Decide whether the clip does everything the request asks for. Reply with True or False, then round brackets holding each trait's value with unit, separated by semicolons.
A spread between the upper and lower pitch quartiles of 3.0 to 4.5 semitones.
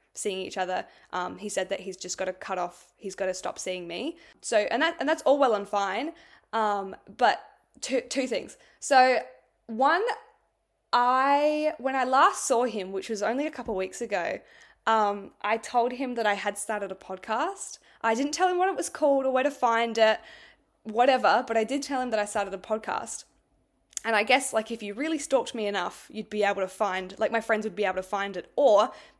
False (4.9 semitones)